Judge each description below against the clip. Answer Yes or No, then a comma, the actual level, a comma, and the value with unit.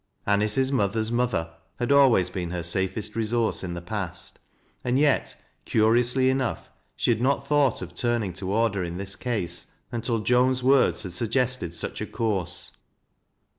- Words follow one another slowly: No, average, 160 wpm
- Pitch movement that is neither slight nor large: Yes, average, 4.8 semitones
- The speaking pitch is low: Yes, low, 110 Hz